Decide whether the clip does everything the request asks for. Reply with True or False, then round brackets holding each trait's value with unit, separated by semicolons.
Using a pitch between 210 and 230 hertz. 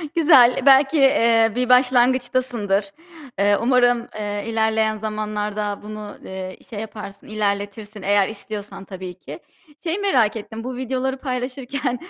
True (225 Hz)